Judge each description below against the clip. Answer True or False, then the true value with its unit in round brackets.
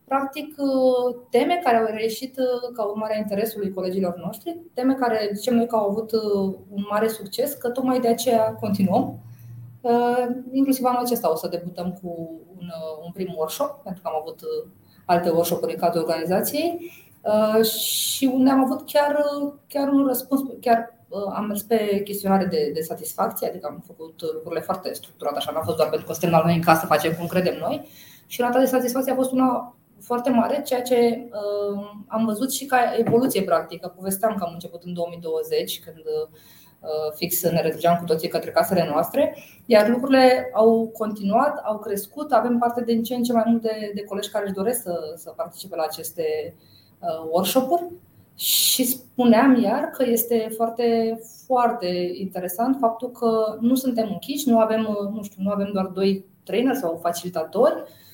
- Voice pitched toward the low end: False (220 Hz)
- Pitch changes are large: True (5.9 semitones)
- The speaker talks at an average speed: False (175 wpm)